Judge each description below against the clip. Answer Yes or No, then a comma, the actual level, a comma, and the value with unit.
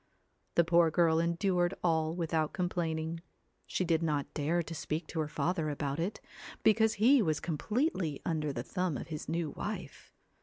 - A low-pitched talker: No, medium, 165 Hz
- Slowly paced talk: No, average, 165 wpm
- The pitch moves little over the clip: Yes, narrow, 2.2 semitones